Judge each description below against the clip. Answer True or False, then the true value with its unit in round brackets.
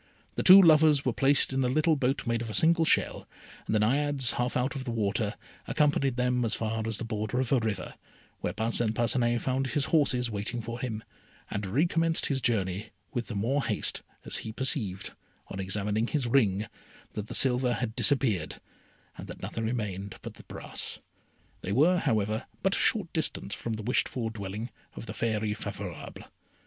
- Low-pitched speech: True (120 Hz)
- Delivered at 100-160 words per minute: False (190 wpm)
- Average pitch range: True (4.0 semitones)